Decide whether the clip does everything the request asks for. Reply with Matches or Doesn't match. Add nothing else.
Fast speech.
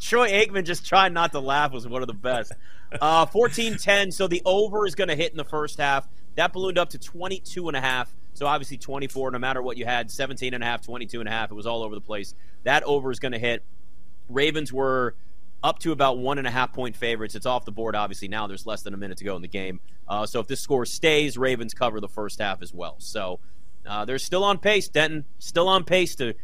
Matches